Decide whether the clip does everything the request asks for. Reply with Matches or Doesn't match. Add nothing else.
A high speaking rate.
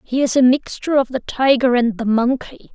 Matches